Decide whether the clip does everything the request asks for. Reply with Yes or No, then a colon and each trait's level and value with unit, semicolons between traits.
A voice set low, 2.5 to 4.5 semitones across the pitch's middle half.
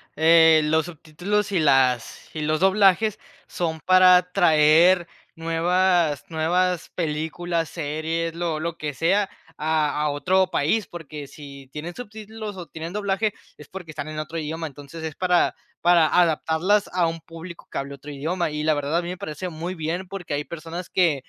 No: medium, 165 Hz; average, 2.8 semitones